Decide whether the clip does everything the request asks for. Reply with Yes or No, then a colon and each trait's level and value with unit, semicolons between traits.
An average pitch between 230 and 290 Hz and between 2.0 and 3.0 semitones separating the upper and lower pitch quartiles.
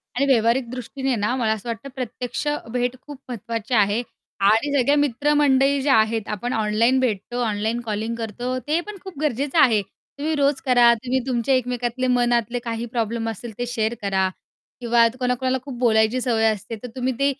Yes: high, 245 Hz; average, 2.7 semitones